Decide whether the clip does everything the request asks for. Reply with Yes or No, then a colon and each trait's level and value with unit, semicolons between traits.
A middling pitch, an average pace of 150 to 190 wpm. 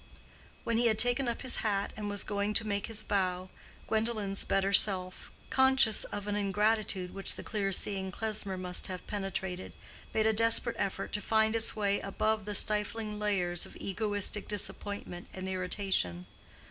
No: high, 205 Hz; average, 165 wpm